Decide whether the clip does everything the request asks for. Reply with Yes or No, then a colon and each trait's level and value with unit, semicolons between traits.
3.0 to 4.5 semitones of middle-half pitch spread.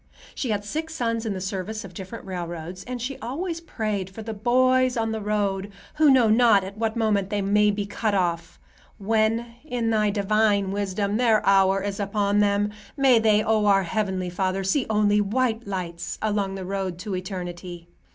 No: narrow, 2.6 semitones